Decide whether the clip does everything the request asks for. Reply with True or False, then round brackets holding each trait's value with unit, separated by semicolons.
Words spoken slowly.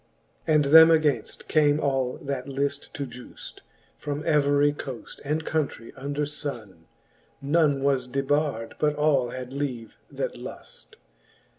True (130 wpm)